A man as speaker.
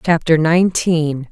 No: female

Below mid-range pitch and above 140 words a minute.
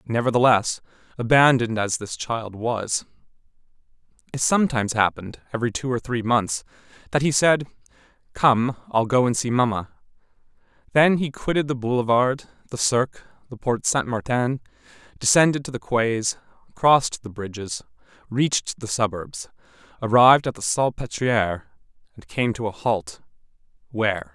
No: low, 120 Hz; slow, 135 wpm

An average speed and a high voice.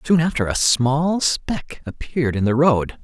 No: average, 180 wpm; medium, 140 Hz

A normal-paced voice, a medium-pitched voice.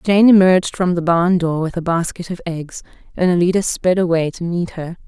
No: fast, 215 wpm; medium, 175 Hz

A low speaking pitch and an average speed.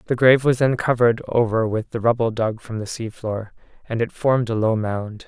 No: low, 115 Hz; fast, 215 wpm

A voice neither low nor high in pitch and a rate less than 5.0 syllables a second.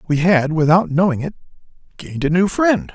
No: medium, 165 Hz; 5.6 syllables/s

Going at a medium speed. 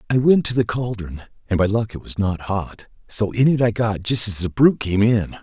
No: fast, 255 wpm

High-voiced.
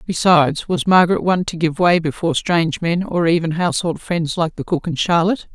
No: medium, 170 Hz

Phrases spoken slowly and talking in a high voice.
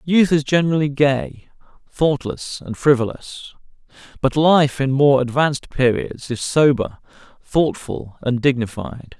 No: slow, 115 wpm; medium, 140 Hz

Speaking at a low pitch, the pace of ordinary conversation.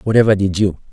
Yes: low, 100 Hz; average, 195 wpm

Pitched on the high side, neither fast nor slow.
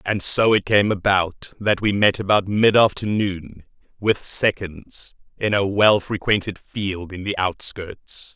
No: low, 100 Hz; average, 150 wpm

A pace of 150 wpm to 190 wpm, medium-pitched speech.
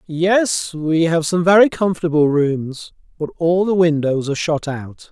Yes: average, 165 wpm; medium, 165 Hz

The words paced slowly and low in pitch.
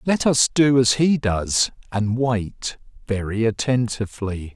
Yes: slow, 130 wpm; low, 115 Hz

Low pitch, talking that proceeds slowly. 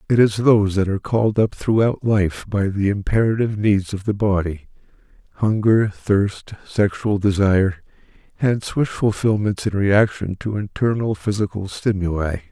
Yes: low, 100 Hz; slow, 130 wpm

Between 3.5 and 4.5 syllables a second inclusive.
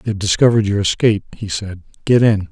No: 6.0 syllables/s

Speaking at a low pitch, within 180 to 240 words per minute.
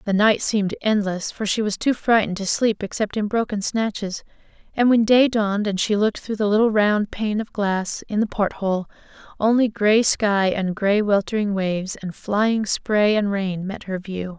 No: high, 205 Hz; average, 200 wpm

